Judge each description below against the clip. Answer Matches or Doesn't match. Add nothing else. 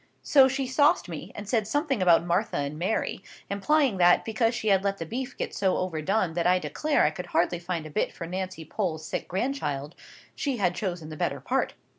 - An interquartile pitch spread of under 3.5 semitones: Doesn't match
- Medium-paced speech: Doesn't match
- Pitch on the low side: Doesn't match